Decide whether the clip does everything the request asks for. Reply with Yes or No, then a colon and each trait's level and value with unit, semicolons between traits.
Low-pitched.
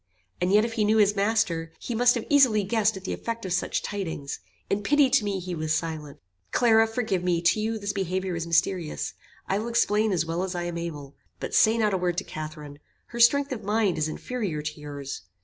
No: high, 195 Hz